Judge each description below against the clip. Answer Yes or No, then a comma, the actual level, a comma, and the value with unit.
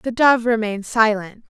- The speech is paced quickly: No, average, 150 wpm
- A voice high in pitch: Yes, high, 225 Hz